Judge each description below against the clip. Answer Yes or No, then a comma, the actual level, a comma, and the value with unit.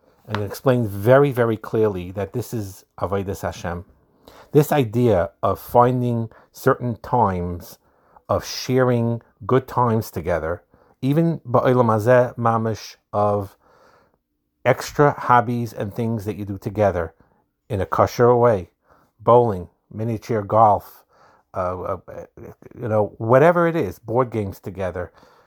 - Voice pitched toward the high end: No, low, 115 Hz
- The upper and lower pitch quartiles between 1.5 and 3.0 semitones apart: No, average, 3.6 semitones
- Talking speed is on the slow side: Yes, slow, 115 wpm